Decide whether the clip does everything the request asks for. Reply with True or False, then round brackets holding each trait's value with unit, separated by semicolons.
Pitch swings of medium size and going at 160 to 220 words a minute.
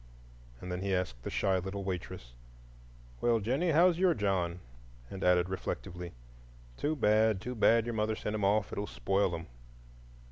True (3.6 semitones; 165 wpm)